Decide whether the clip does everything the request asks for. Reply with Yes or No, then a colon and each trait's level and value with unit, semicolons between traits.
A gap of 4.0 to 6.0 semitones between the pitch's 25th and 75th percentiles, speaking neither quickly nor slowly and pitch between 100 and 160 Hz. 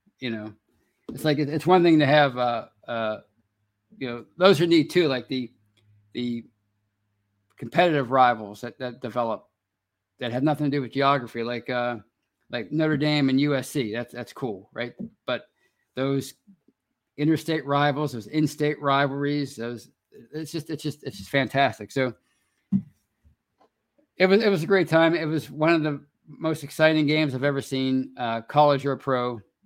Yes: average, 4.4 semitones; average, 165 wpm; low, 135 Hz